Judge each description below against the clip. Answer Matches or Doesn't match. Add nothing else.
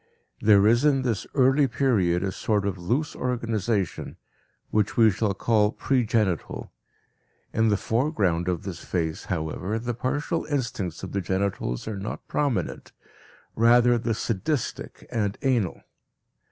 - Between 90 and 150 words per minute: Matches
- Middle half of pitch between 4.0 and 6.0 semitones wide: Matches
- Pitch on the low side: Matches